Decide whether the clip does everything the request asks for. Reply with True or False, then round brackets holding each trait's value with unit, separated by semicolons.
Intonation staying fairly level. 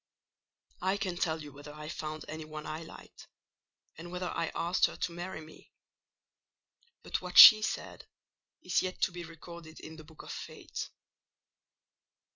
True (2.3 semitones)